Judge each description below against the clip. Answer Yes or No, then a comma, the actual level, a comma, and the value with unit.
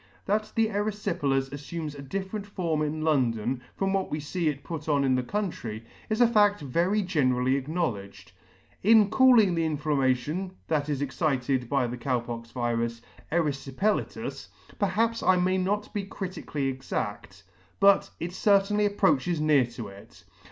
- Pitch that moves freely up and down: Yes, wide, 7.0 semitones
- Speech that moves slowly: No, average, 155 wpm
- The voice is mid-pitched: Yes, medium, 155 Hz